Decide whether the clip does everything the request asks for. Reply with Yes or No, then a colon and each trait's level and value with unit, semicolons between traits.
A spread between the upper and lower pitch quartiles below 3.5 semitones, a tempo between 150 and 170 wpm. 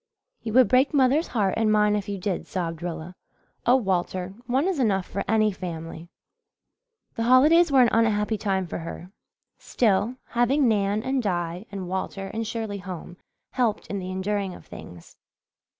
No: average, 4.4 semitones; average, 165 wpm